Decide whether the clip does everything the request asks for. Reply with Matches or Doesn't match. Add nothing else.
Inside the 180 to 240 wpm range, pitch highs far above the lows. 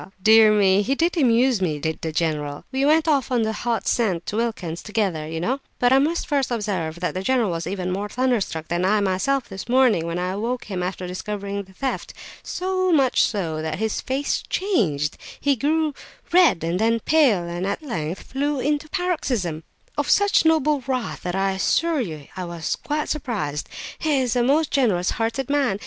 Matches